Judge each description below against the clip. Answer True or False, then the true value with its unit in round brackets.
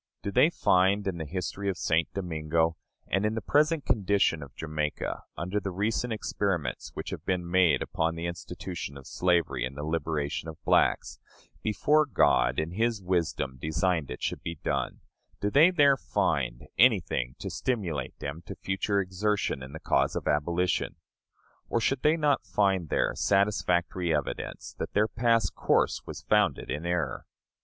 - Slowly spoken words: False (165 wpm)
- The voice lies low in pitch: True (90 Hz)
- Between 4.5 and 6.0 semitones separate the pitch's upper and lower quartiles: True (4.8 semitones)